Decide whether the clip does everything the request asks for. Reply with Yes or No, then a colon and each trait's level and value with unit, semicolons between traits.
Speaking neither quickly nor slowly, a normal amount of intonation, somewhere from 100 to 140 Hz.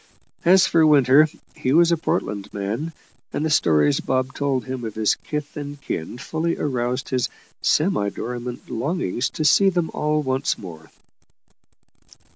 Yes: average, 150 wpm; average, 4.6 semitones; low, 135 Hz